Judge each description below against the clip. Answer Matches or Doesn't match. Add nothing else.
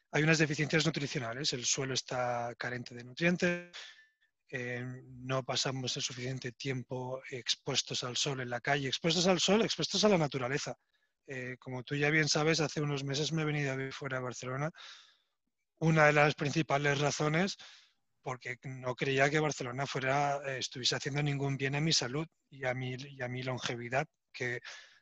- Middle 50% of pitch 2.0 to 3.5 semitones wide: Matches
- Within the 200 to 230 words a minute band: Doesn't match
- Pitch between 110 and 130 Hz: Doesn't match